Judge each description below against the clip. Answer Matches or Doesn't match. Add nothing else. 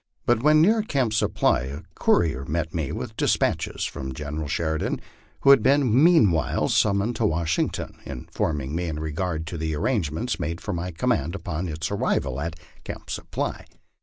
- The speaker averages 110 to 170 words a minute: Matches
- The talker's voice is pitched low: Matches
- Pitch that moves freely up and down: Matches